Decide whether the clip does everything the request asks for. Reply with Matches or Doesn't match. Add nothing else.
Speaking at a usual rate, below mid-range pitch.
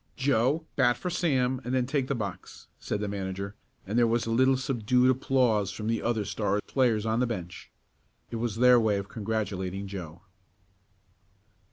Matches